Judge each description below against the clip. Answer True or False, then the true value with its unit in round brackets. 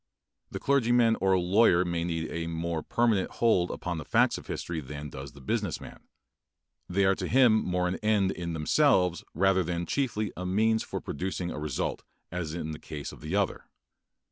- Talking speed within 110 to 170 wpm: False (190 wpm)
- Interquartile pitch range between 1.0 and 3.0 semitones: False (4.4 semitones)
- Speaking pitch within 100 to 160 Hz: False (90 Hz)